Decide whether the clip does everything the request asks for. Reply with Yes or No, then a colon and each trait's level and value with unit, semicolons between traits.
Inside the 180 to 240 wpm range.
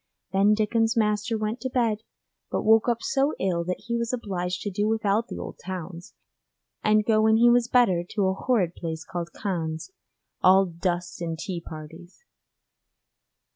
No: average, 170 wpm